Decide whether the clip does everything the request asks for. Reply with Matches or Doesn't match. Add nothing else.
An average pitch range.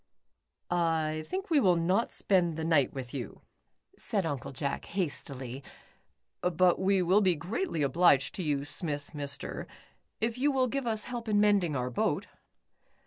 Doesn't match